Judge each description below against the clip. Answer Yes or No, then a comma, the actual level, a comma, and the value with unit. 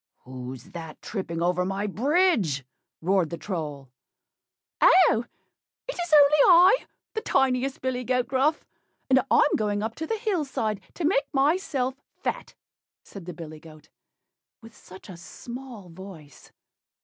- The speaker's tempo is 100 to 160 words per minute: Yes, average, 140 wpm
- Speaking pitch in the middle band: No, high, 220 Hz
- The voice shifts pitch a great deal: Yes, wide, 8.7 semitones